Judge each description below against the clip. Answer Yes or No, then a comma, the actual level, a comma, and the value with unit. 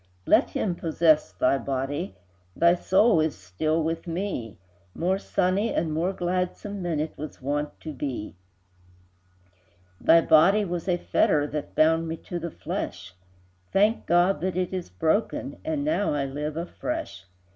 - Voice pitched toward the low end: No, medium, 165 Hz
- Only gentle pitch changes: No, average, 3.7 semitones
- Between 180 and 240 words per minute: No, average, 150 wpm